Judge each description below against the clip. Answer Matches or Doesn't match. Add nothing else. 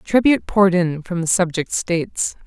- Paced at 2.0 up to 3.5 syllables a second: Doesn't match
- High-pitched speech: Doesn't match